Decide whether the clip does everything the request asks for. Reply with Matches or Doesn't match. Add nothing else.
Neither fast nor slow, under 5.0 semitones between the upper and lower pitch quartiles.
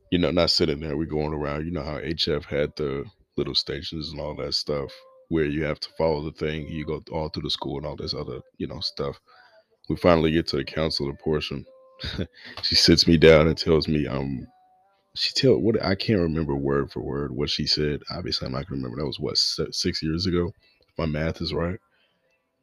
Doesn't match